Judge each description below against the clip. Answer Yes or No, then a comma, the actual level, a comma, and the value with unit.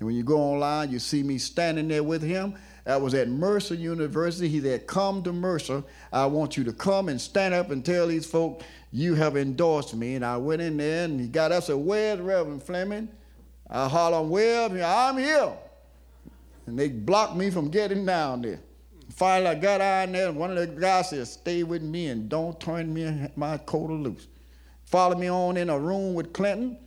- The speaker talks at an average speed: No, fast, 210 wpm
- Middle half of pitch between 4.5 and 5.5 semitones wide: Yes, average, 4.8 semitones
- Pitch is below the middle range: No, medium, 165 Hz